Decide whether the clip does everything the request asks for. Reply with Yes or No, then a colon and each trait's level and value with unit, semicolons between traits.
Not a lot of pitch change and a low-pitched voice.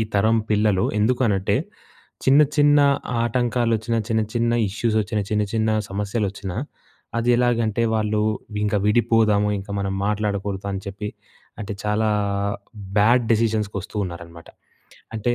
Yes: narrow, 2.3 semitones; low, 110 Hz